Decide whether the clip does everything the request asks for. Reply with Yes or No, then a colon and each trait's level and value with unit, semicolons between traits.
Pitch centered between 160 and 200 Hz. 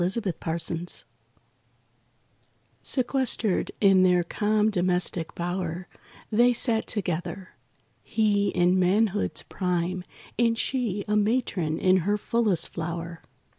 Yes: medium, 185 Hz